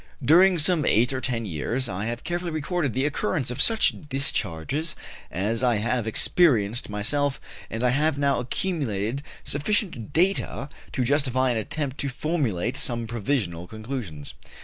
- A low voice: Yes, low, 130 Hz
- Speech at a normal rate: Yes, average, 150 wpm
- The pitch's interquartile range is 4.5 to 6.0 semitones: Yes, average, 4.9 semitones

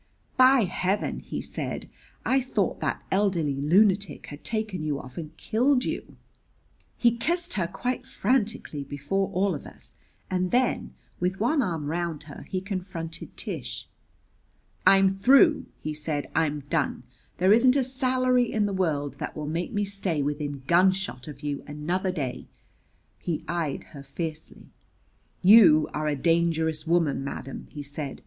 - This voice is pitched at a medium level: Yes, medium, 175 Hz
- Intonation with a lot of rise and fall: Yes, wide, 5.9 semitones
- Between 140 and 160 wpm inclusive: Yes, average, 150 wpm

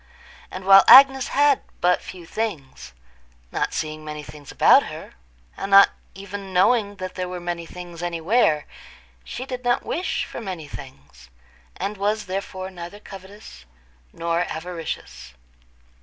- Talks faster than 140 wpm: No, slow, 135 wpm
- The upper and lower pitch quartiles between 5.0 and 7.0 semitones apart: No, average, 4.6 semitones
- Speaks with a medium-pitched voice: Yes, medium, 180 Hz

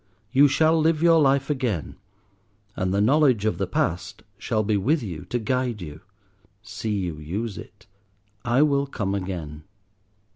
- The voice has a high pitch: No, low, 110 Hz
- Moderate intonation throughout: No, wide, 6.8 semitones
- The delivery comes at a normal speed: Yes, average, 155 wpm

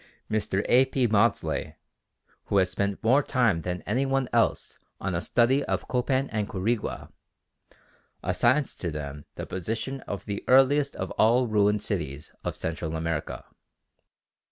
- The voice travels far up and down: Yes, wide, 5.7 semitones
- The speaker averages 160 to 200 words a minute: No, average, 145 wpm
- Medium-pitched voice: No, low, 105 Hz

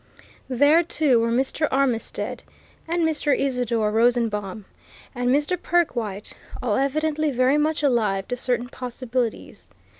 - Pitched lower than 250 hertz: No, very high, 255 Hz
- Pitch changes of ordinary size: Yes, average, 4.2 semitones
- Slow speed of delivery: Yes, slow, 120 wpm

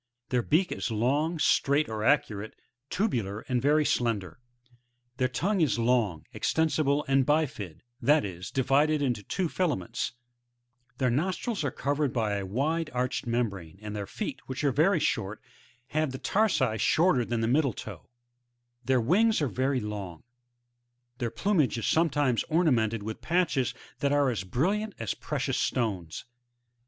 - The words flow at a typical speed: Yes, average, 150 wpm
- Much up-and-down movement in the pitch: Yes, wide, 5.8 semitones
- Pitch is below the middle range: Yes, low, 130 Hz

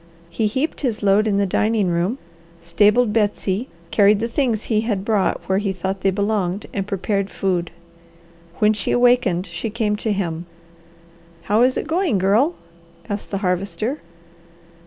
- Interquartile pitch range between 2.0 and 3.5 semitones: Yes, narrow, 2.6 semitones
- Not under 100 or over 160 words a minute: Yes, average, 155 wpm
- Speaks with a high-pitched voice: Yes, high, 205 Hz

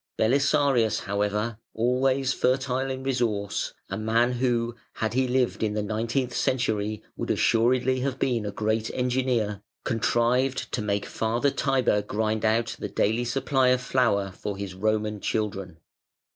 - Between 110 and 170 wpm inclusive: Yes, average, 145 wpm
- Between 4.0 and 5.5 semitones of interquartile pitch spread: No, average, 3.3 semitones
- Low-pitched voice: Yes, low, 115 Hz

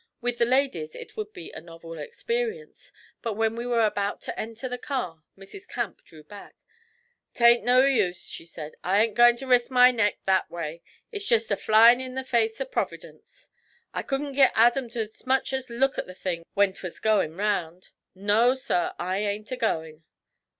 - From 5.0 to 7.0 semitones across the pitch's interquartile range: Yes, average, 5.3 semitones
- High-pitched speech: Yes, high, 225 Hz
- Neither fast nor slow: Yes, average, 190 wpm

